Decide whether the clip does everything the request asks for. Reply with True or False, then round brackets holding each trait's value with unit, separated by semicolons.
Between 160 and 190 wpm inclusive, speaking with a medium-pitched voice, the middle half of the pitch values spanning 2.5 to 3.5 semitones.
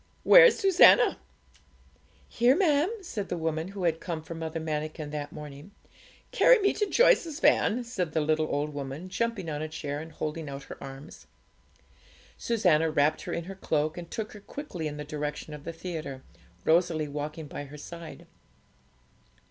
False (170 wpm; 160 Hz; 5.1 semitones)